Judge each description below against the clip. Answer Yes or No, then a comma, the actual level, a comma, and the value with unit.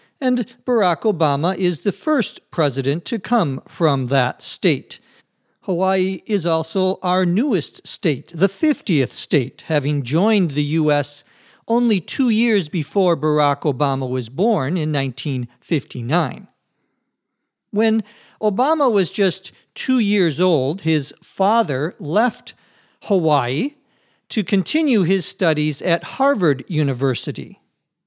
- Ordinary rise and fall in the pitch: No, wide, 6.3 semitones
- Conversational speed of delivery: No, slow, 115 wpm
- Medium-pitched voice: Yes, medium, 180 Hz